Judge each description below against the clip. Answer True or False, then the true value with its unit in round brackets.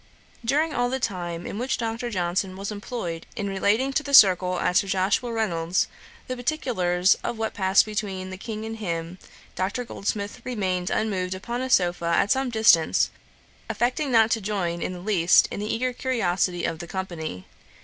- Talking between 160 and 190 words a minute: True (180 wpm)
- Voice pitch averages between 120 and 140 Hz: False (200 Hz)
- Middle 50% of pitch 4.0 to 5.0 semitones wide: True (4.4 semitones)